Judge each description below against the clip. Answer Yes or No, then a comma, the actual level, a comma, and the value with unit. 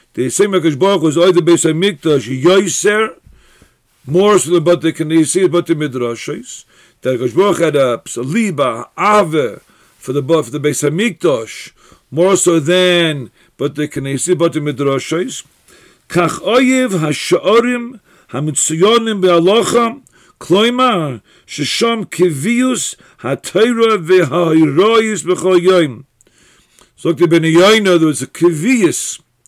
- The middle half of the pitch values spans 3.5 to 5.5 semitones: Yes, average, 4.8 semitones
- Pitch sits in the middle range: Yes, medium, 175 Hz